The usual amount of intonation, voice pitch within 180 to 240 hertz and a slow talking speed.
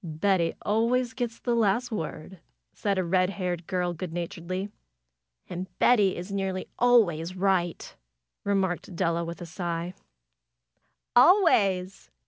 Yes: average, 3.0 semitones; medium, 185 Hz; slow, 120 wpm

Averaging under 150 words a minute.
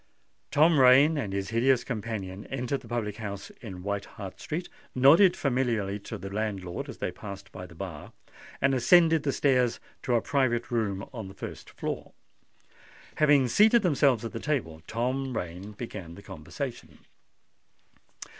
No: average, 155 wpm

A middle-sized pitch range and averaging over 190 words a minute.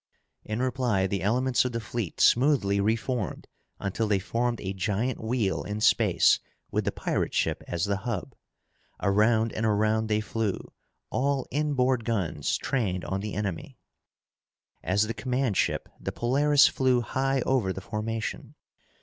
No: average, 4.0 semitones; average, 150 wpm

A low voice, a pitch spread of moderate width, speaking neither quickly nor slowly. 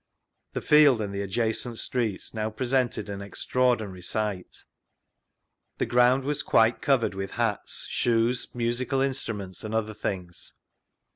No: low, 115 Hz; average, 3.6 semitones; slow, 130 wpm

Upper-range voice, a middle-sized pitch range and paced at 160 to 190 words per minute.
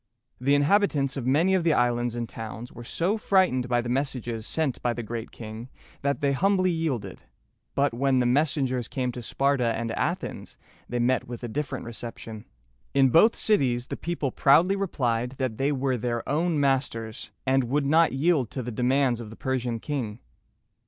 No: low, 130 Hz; average, 3.4 semitones; average, 180 wpm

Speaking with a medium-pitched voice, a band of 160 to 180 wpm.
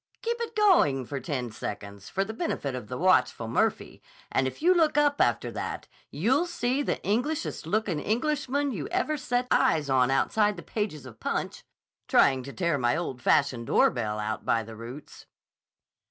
Yes: medium, 165 Hz; average, 175 wpm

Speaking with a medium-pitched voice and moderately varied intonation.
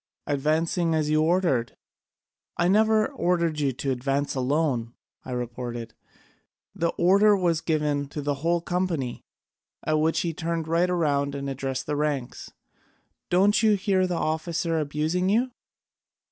Yes: medium, 160 Hz; average, 4.0 semitones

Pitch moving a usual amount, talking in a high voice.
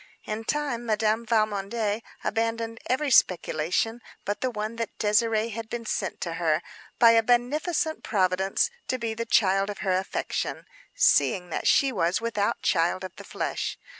Yes: average, 3.1 semitones; high, 220 Hz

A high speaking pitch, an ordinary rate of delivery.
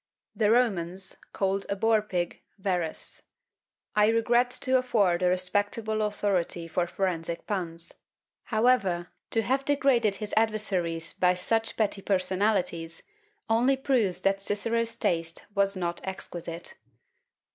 No: high, 200 Hz; slow, 120 wpm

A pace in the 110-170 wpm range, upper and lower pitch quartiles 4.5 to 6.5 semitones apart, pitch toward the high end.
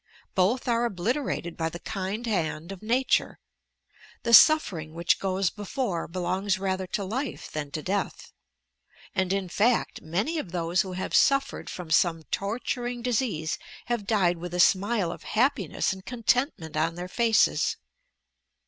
Yes: average, 150 wpm; average, 5.2 semitones; high, 195 Hz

